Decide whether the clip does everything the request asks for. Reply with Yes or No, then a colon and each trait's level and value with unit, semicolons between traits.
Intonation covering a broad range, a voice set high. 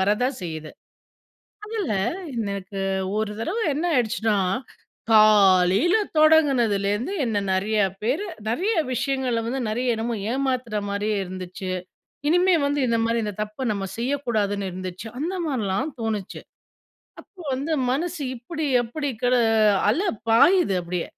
Yes: wide, 5.8 semitones; high, 230 Hz